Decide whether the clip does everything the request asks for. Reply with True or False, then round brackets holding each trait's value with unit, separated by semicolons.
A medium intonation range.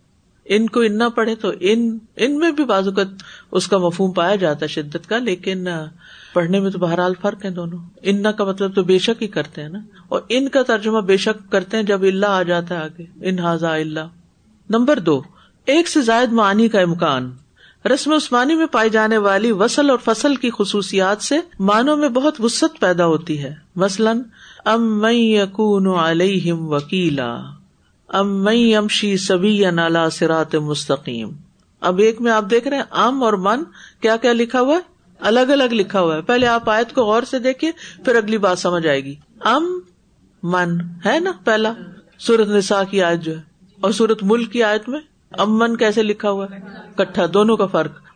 True (4.4 semitones)